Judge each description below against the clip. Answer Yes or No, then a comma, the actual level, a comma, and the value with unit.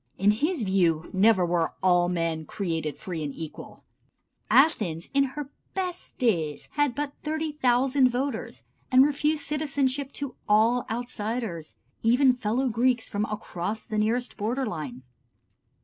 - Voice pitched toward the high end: Yes, high, 230 Hz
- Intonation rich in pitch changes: Yes, wide, 7.2 semitones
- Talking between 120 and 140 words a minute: Yes, slow, 135 wpm